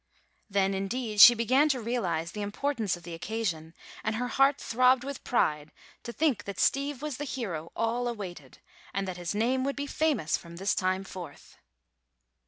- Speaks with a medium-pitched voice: No, high, 220 Hz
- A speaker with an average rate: Yes, average, 180 wpm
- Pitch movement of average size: No, wide, 5.7 semitones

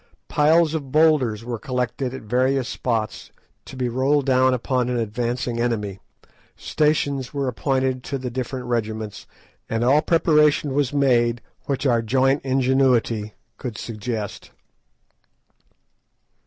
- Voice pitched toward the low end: Yes, low, 130 Hz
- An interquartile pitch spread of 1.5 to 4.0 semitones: Yes, average, 2.7 semitones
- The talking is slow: Yes, slow, 125 wpm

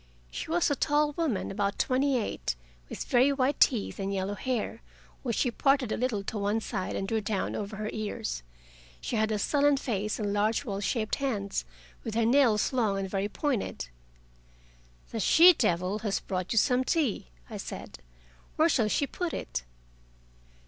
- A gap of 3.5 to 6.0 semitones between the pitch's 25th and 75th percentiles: Yes, average, 5.0 semitones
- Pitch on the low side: No, high, 220 Hz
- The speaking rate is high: No, average, 175 wpm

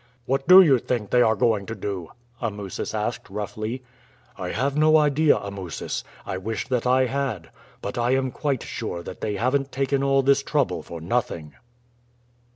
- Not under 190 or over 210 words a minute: No, average, 170 wpm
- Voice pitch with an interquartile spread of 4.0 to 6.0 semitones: Yes, average, 5.2 semitones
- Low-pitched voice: Yes, low, 120 Hz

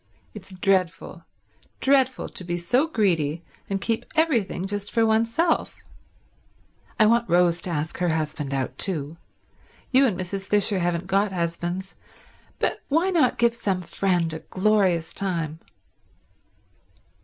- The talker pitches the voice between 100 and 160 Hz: No, high, 190 Hz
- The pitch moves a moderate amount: Yes, average, 4.6 semitones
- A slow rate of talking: Yes, slow, 130 wpm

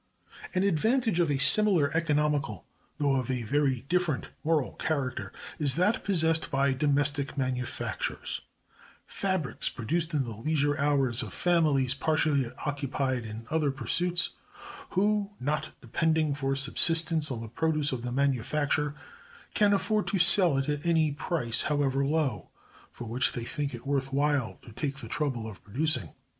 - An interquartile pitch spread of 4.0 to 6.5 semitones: No, average, 3.5 semitones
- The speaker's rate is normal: Yes, average, 150 wpm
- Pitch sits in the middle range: Yes, medium, 145 Hz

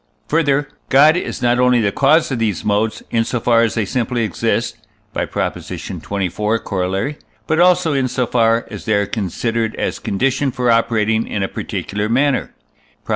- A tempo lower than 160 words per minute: No, average, 180 wpm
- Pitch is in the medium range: No, low, 115 Hz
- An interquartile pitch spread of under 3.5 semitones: No, average, 4.0 semitones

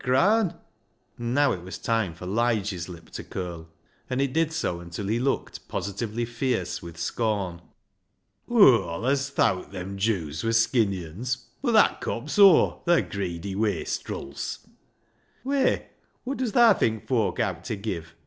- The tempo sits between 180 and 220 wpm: No, average, 165 wpm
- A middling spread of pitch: No, wide, 6.7 semitones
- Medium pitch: No, low, 110 Hz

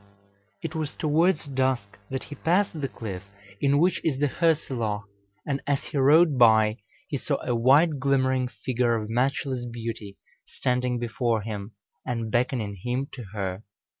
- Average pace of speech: Yes, average, 155 wpm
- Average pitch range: Yes, average, 4.0 semitones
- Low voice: Yes, low, 125 Hz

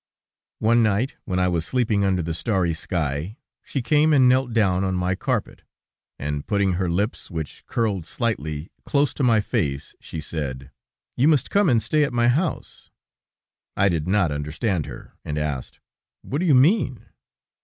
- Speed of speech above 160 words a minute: Yes, average, 170 wpm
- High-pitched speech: No, low, 100 Hz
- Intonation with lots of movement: Yes, wide, 7.3 semitones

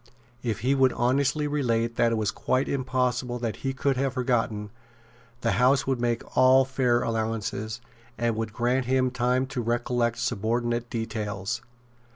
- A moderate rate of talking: Yes, average, 155 wpm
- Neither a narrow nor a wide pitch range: No, narrow, 2.2 semitones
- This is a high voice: No, low, 120 Hz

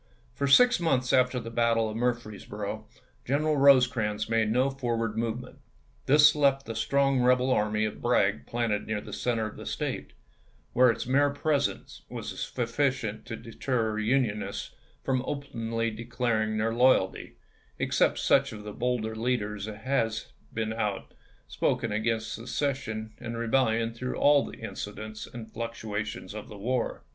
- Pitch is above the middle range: No, low, 115 Hz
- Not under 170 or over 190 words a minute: No, average, 150 wpm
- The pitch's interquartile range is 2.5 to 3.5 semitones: Yes, average, 2.9 semitones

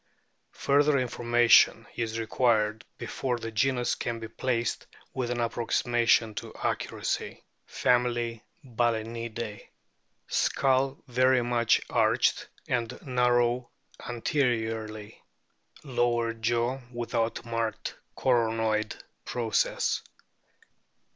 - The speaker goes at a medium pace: No, slow, 90 wpm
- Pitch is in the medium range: No, low, 120 Hz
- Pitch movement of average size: No, narrow, 1.4 semitones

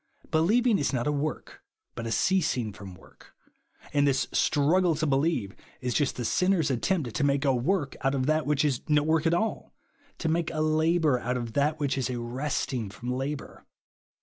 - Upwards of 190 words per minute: Yes, average, 200 wpm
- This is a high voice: No, medium, 145 Hz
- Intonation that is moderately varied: Yes, average, 3.9 semitones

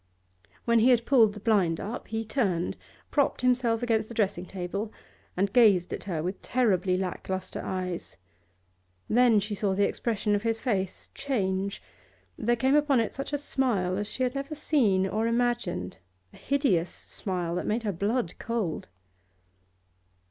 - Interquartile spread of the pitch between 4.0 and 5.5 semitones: Yes, average, 4.3 semitones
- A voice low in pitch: No, high, 215 Hz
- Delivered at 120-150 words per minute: No, average, 165 wpm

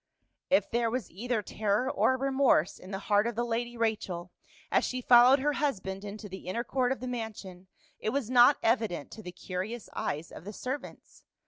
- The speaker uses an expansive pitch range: No, average, 4.4 semitones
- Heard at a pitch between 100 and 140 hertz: No, high, 225 Hz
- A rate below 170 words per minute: No, average, 195 wpm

